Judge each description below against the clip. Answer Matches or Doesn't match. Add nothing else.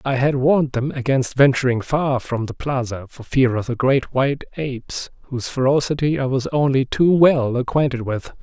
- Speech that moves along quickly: Doesn't match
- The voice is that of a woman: Doesn't match